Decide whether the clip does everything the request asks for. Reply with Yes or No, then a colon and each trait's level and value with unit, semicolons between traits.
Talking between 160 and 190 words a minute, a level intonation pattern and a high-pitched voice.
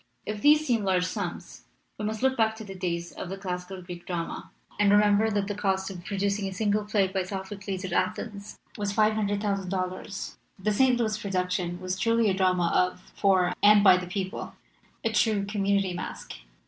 Yes: average, 185 wpm; narrow, 2.3 semitones; high, 195 Hz